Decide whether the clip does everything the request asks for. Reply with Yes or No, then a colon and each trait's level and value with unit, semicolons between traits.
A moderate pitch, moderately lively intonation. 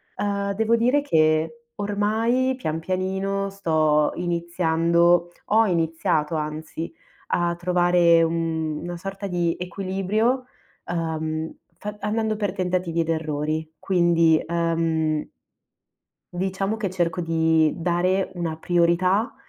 Yes: medium, 175 Hz; average, 3.3 semitones